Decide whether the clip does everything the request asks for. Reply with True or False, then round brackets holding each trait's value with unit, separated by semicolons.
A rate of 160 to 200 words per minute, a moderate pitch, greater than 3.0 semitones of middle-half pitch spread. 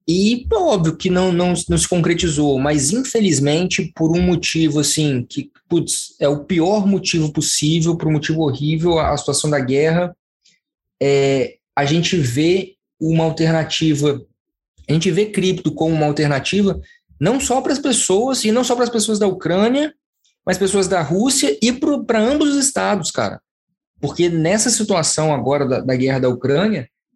True (165 wpm; 170 Hz; 5.3 semitones)